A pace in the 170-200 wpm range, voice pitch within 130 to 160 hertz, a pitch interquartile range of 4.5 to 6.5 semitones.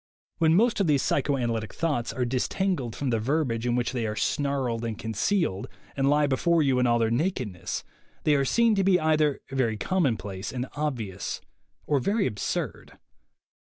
Yes: average, 180 wpm; low, 135 Hz; average, 5.2 semitones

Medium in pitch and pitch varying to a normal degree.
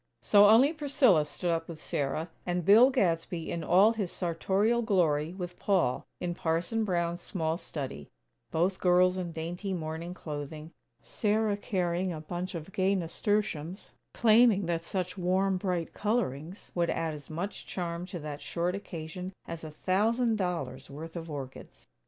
Yes: medium, 175 Hz; average, 3.3 semitones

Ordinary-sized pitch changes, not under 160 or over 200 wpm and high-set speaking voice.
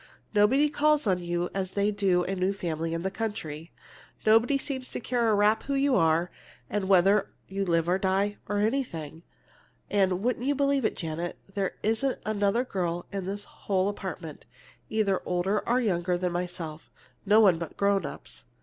Yes: average, 3.7 semitones; average, 180 wpm; high, 195 Hz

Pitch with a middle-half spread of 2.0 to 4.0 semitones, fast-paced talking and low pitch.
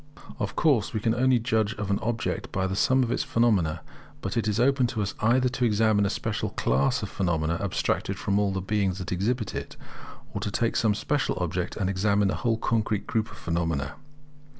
Yes: average, 3.4 semitones; fast, 210 wpm; low, 105 Hz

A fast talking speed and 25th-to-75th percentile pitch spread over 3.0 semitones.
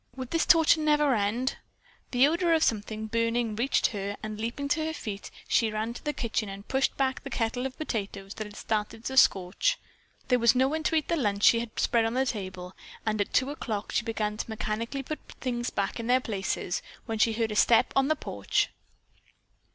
Yes: fast, 215 wpm; average, 3.9 semitones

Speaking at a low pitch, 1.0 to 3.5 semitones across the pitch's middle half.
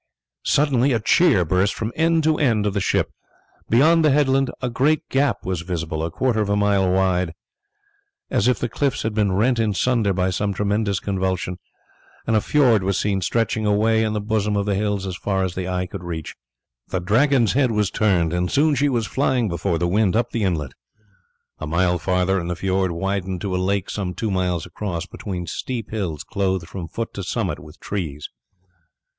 No: low, 100 Hz; average, 3.9 semitones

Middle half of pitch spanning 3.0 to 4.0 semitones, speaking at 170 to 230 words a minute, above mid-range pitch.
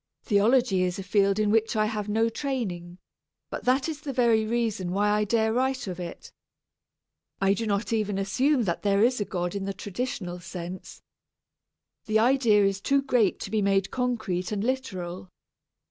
Yes: average, 3.6 semitones; average, 180 wpm; high, 210 Hz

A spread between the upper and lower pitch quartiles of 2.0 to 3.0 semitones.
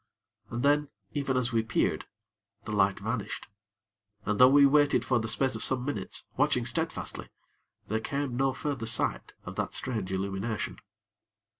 No: average, 4.1 semitones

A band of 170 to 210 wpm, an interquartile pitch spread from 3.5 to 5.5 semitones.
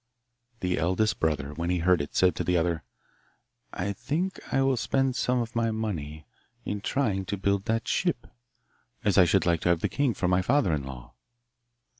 Yes: average, 195 wpm; average, 5.2 semitones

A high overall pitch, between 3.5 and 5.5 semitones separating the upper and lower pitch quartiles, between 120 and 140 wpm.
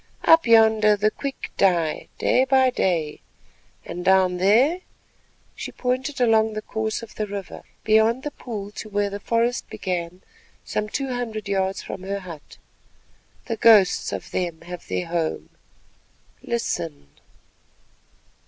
Yes: high, 210 Hz; average, 3.9 semitones; slow, 135 wpm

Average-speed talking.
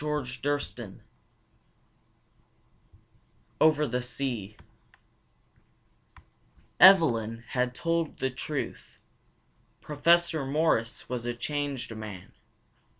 No: slow, 75 wpm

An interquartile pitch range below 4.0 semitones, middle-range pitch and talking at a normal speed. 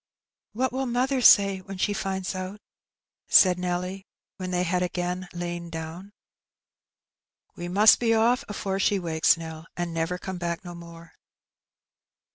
Yes: narrow, 2.4 semitones; medium, 180 Hz; average, 160 wpm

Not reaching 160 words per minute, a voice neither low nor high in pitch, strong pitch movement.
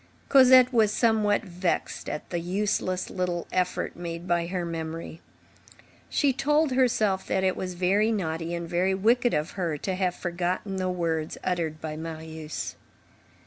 No: average, 150 wpm; medium, 180 Hz; average, 3.7 semitones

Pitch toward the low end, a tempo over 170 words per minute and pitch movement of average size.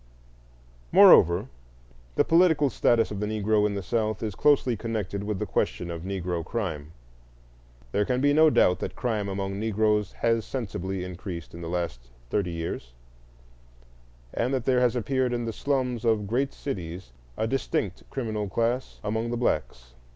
No: low, 105 Hz; average, 160 wpm; average, 4.6 semitones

